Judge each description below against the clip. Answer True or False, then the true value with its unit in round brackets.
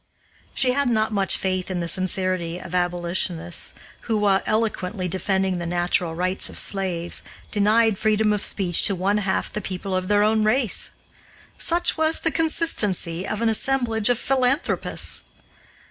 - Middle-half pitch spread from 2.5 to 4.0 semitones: True (3.4 semitones)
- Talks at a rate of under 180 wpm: True (155 wpm)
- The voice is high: True (195 Hz)